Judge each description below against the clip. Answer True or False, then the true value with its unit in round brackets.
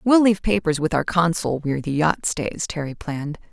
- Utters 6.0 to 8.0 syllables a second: False (5.5 syllables/s)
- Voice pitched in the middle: True (165 Hz)